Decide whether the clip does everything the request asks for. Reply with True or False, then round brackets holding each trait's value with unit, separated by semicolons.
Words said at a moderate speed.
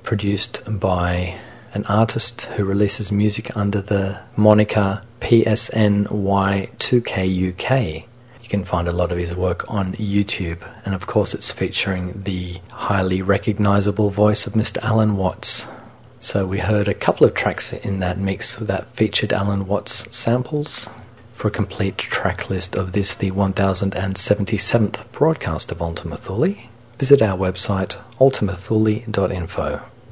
False (130 wpm)